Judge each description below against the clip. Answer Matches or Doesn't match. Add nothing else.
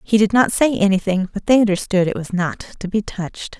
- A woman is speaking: Matches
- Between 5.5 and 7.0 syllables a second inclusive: Matches